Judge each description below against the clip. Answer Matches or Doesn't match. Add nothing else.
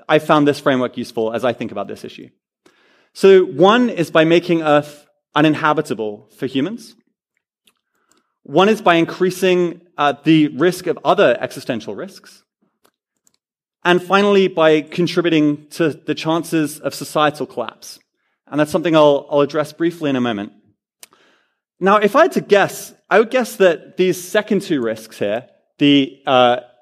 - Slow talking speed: Doesn't match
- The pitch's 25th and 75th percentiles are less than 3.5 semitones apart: Doesn't match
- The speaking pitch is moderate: Matches